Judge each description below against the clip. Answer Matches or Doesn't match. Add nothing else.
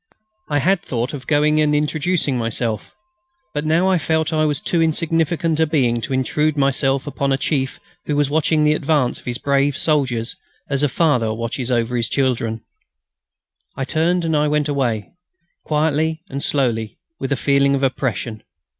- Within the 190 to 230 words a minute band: Doesn't match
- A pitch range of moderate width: Matches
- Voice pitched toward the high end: Doesn't match